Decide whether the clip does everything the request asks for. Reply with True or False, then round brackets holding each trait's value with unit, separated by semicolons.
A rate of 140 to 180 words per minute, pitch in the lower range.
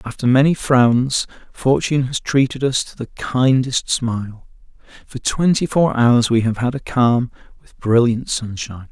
True (150 wpm; 125 Hz)